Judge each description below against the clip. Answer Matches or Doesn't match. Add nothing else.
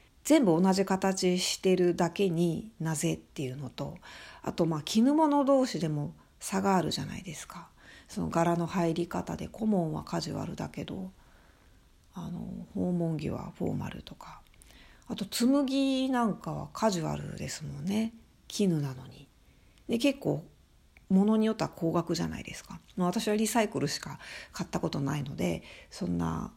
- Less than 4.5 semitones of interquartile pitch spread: Doesn't match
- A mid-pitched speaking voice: Matches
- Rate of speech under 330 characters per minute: Matches